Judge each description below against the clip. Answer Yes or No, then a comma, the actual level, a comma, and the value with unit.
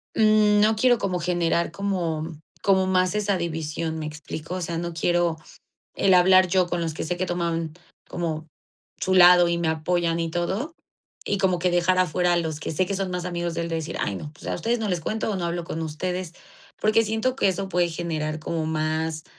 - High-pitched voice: No, medium, 175 Hz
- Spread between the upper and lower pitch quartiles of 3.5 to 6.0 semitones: No, narrow, 2.4 semitones